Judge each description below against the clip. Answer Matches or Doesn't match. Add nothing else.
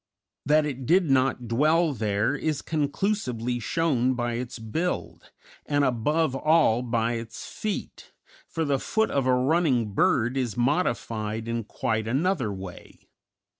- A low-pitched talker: Matches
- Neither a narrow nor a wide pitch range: Matches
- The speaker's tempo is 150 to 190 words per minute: Doesn't match